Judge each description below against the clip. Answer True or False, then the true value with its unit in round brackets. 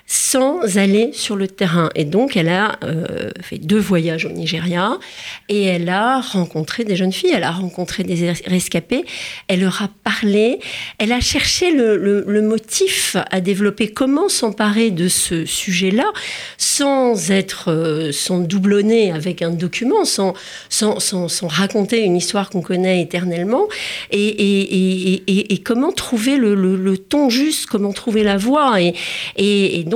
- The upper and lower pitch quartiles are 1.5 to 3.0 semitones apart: False (4.0 semitones)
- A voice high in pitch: True (200 Hz)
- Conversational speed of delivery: True (170 wpm)